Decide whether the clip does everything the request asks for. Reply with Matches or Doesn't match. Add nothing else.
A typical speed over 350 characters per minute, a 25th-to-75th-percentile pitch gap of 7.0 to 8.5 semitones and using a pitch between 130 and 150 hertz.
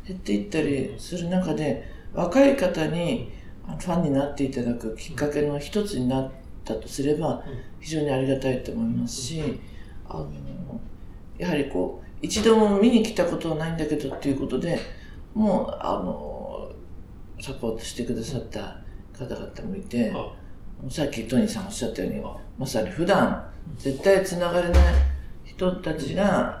Doesn't match